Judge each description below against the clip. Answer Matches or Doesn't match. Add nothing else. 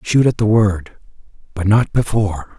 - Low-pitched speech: Matches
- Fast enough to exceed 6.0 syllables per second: Doesn't match